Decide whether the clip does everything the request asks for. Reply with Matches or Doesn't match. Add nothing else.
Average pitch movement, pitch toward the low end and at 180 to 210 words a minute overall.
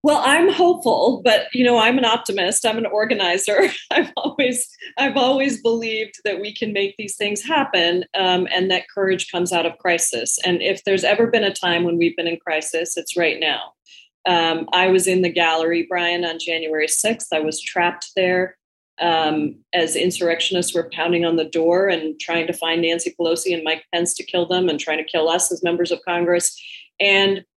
Doesn't match